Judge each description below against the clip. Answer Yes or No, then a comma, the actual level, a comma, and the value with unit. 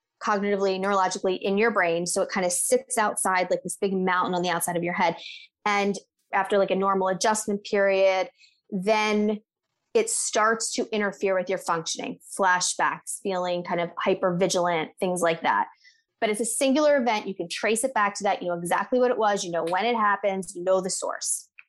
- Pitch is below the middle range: No, high, 195 Hz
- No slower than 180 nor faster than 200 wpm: Yes, average, 195 wpm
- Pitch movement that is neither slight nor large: Yes, average, 3.1 semitones